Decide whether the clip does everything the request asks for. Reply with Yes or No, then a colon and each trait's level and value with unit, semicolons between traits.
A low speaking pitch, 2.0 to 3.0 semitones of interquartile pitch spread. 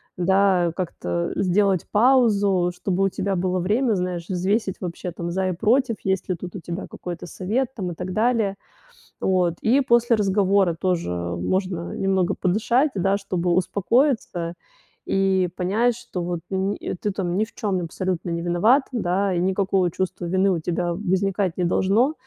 No: high, 190 Hz; narrow, 2.6 semitones